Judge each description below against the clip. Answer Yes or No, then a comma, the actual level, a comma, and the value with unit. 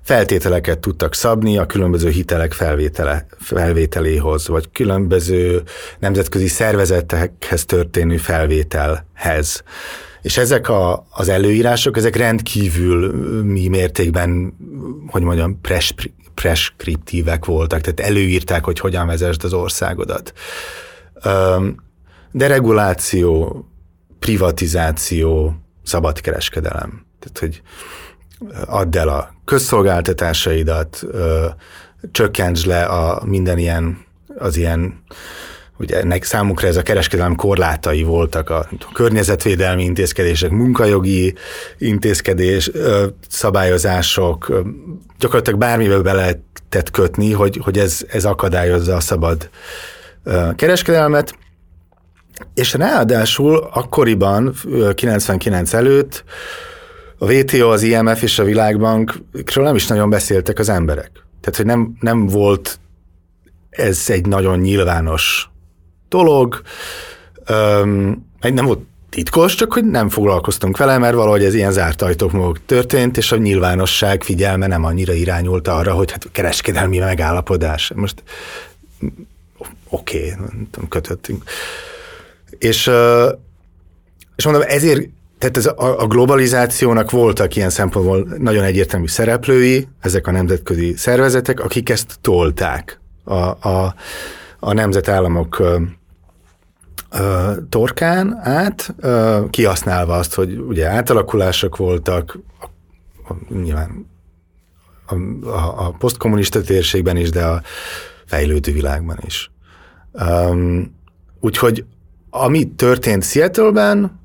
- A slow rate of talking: Yes, slow, 100 wpm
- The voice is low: Yes, very low, 95 Hz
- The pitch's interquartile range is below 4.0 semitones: No, average, 4.4 semitones